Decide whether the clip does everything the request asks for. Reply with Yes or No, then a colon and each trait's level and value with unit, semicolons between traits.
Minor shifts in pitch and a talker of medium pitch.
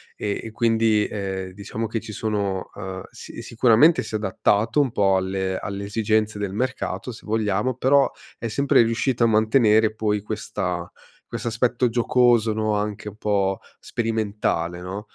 No: narrow, 2.3 semitones; low, 110 Hz